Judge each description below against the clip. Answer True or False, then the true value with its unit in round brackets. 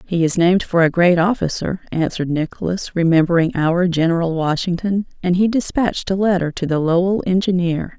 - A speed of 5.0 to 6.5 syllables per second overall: True (5.5 syllables/s)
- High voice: False (175 Hz)